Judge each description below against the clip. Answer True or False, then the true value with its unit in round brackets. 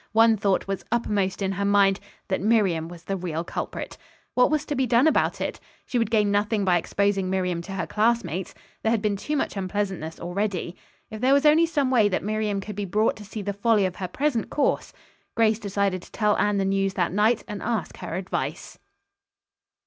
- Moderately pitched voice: False (205 Hz)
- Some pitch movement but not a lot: True (3.0 semitones)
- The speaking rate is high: True (210 wpm)